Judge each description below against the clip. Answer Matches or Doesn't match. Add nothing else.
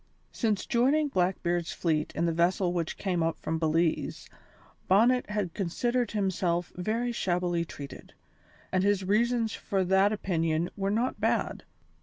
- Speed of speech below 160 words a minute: Matches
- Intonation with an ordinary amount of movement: Matches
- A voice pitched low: Doesn't match